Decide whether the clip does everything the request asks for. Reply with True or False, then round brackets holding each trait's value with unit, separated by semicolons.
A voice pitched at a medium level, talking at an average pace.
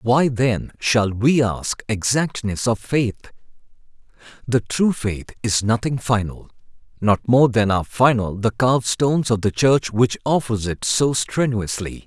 False (115 Hz; 150 wpm)